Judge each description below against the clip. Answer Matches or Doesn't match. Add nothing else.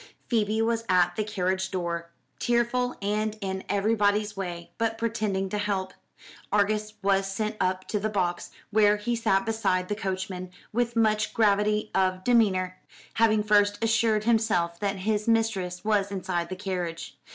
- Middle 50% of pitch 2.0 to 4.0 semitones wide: Matches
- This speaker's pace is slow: Doesn't match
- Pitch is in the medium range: Doesn't match